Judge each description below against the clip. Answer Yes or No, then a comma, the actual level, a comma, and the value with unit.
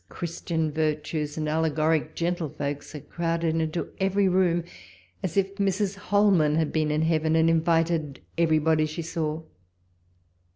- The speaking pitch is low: No, medium, 160 Hz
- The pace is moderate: No, slow, 130 wpm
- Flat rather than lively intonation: Yes, narrow, 1.9 semitones